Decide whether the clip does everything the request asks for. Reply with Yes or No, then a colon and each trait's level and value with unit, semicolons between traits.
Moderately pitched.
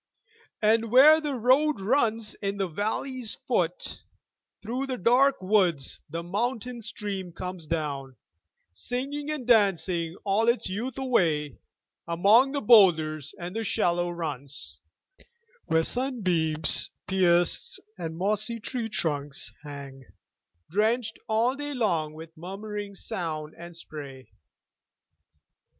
No: high, 195 Hz